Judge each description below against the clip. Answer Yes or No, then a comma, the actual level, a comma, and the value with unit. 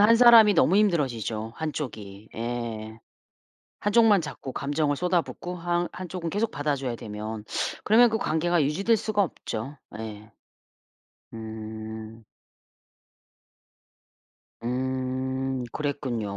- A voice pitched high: No, low, 135 Hz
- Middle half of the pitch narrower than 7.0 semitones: No, wide, 7.9 semitones